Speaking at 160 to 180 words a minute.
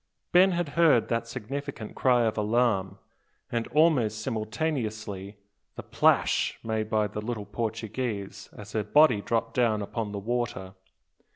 No: slow, 135 wpm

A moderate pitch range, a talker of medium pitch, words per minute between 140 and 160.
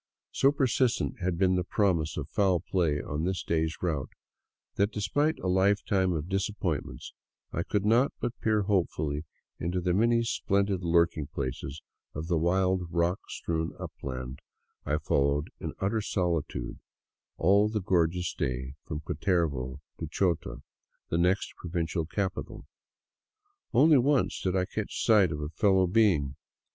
No: average, 4.1 semitones; very low, 90 Hz; average, 150 wpm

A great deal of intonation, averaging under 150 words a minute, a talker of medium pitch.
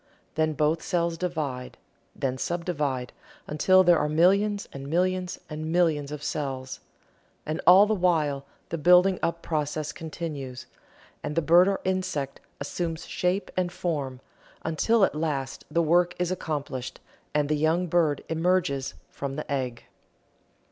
No: average, 3.7 semitones; average, 140 wpm; medium, 160 Hz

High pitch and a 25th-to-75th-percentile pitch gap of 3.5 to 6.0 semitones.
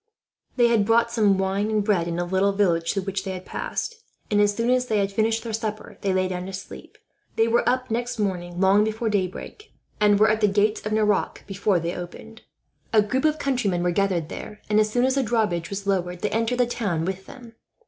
No: high, 205 Hz; average, 3.1 semitones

